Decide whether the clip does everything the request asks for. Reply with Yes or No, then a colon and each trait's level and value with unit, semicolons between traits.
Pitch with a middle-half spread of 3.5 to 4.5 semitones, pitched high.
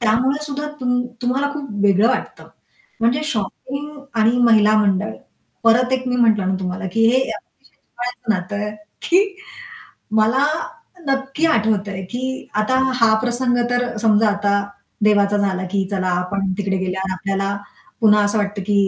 Yes: average, 4.0 semitones; high, 220 Hz